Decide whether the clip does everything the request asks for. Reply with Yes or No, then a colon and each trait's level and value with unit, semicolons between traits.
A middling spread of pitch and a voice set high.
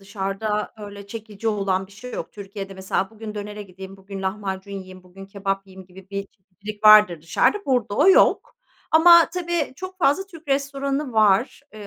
Yes: average, 4.5 semitones; high, 205 Hz